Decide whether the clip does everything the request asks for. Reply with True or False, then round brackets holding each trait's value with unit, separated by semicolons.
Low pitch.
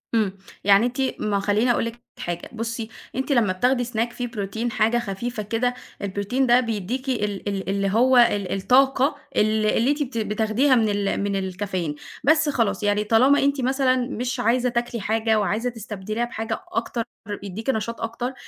False (225 Hz)